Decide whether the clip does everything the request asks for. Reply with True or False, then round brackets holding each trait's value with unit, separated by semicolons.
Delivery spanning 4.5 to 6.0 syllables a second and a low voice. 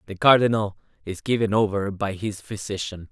True (5.3 syllables/s; 105 Hz)